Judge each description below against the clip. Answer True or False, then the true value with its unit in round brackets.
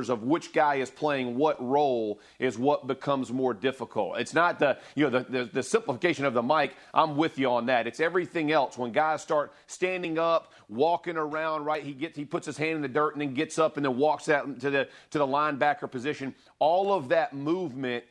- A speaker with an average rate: False (220 wpm)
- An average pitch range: True (3.3 semitones)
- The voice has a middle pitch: True (145 Hz)